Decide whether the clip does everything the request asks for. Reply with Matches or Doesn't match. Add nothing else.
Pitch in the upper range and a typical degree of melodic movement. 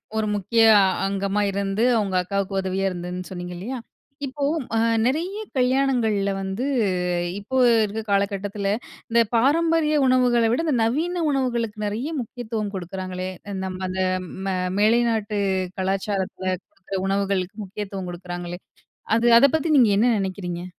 Matches